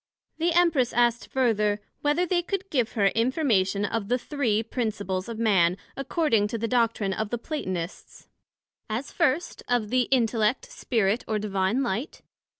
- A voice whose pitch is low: No, high, 230 Hz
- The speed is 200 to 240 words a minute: No, average, 150 wpm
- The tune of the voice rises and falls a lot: No, average, 4.6 semitones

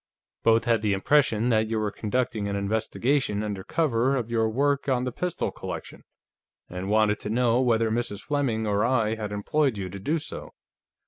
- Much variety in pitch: No, average, 3.4 semitones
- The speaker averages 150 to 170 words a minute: No, average, 185 wpm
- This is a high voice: No, low, 115 Hz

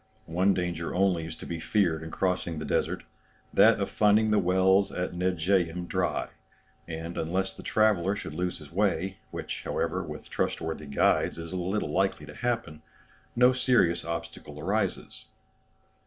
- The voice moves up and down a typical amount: Yes, average, 3.1 semitones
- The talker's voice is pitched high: No, very low, 90 Hz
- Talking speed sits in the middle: Yes, average, 155 wpm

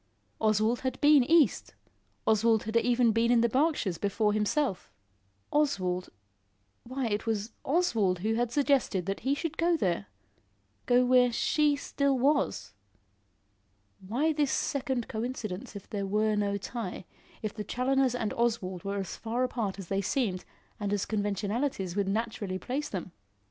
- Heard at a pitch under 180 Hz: No, high, 225 Hz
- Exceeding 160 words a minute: No, average, 150 wpm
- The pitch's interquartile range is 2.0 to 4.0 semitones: No, average, 4.4 semitones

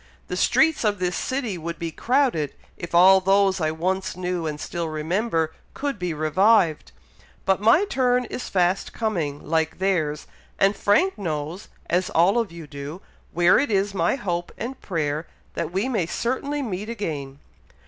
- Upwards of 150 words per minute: Yes, average, 165 wpm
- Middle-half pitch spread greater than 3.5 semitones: Yes, average, 4.9 semitones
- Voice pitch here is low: No, medium, 185 Hz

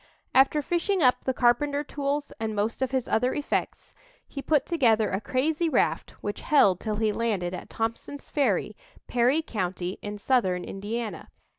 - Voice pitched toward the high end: Yes, high, 240 Hz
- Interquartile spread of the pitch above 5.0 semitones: Yes, wide, 5.4 semitones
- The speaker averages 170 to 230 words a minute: No, average, 160 wpm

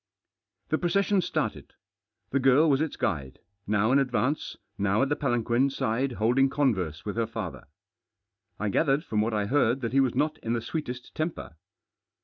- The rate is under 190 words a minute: Yes, average, 170 wpm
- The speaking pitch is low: Yes, low, 125 Hz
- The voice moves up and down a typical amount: Yes, average, 4.4 semitones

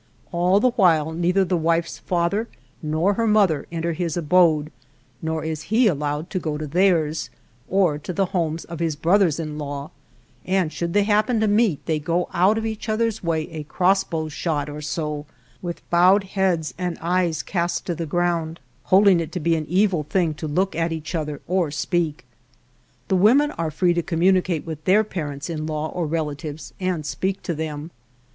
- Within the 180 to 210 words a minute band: Yes, average, 185 wpm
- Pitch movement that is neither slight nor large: Yes, average, 3.2 semitones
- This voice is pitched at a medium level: Yes, medium, 170 Hz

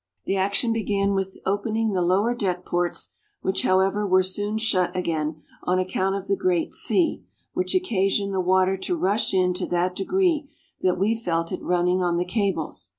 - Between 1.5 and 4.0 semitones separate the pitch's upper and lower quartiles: Yes, narrow, 2.4 semitones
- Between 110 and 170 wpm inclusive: No, average, 180 wpm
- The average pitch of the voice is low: No, high, 190 Hz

